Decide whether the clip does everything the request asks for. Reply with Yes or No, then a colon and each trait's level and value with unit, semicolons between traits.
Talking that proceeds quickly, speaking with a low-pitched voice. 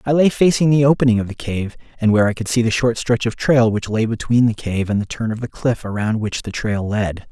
Yes: fast, 280 wpm; low, 115 Hz